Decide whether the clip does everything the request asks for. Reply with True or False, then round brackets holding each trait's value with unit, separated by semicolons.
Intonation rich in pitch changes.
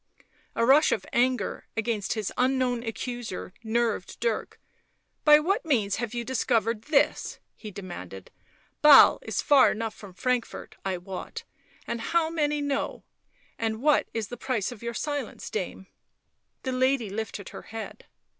False (3.6 semitones)